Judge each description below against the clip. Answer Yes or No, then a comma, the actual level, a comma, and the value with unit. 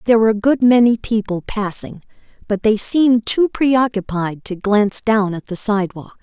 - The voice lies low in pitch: No, high, 215 Hz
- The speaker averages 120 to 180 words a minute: Yes, average, 175 wpm